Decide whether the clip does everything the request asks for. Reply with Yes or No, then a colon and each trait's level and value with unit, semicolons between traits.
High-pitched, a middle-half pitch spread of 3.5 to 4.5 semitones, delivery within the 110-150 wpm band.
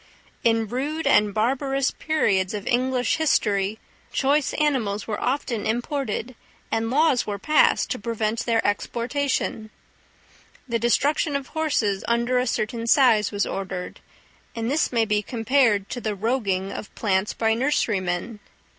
Yes: high, 230 Hz; average, 4.2 semitones; slow, 135 wpm